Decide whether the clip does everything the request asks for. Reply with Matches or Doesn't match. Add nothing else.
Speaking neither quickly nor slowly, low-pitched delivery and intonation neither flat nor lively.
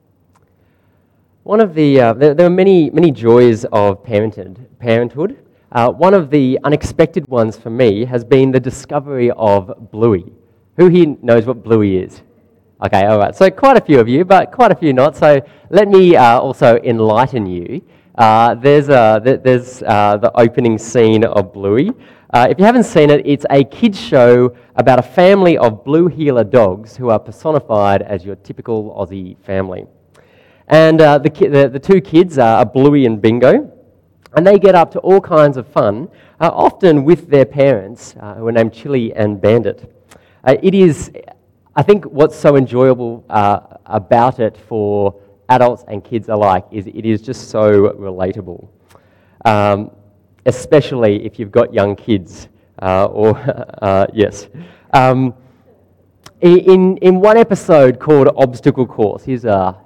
Doesn't match